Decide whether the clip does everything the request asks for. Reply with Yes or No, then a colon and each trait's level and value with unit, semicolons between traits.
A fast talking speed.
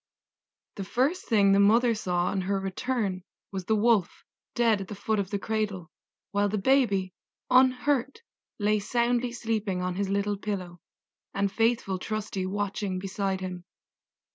No: average, 150 wpm